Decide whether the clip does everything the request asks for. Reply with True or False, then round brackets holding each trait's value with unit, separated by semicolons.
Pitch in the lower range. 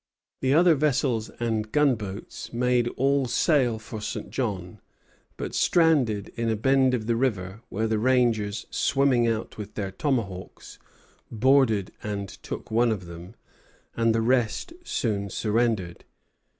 True (115 Hz)